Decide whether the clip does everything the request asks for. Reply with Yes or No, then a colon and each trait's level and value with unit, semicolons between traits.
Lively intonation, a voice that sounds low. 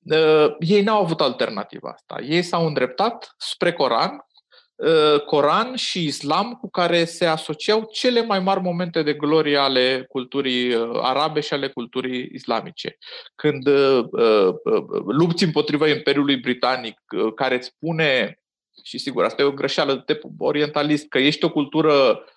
No: wide, 7.0 semitones; medium, 155 Hz